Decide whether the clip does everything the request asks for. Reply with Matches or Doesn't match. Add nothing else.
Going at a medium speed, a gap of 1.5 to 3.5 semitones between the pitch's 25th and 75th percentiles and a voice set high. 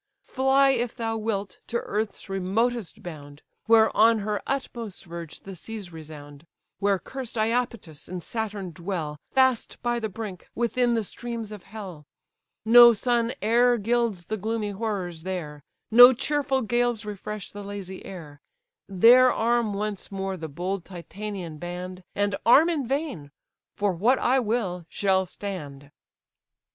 Doesn't match